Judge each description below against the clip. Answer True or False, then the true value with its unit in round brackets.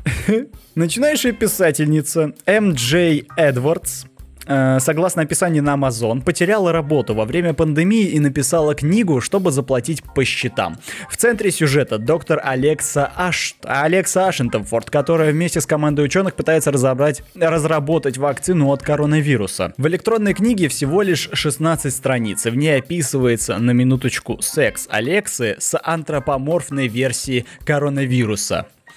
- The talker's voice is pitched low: False (150 Hz)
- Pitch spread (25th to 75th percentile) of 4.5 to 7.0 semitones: False (4.1 semitones)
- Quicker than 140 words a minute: False (120 wpm)